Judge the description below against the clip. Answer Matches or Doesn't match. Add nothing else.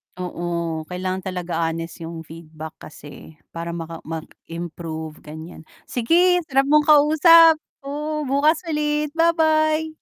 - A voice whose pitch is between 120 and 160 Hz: Doesn't match